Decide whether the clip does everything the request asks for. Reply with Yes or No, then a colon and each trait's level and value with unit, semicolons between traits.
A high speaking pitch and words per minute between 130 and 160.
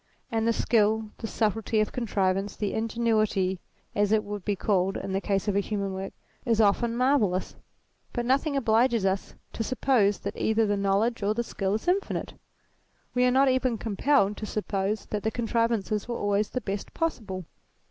No: high, 215 Hz; average, 180 wpm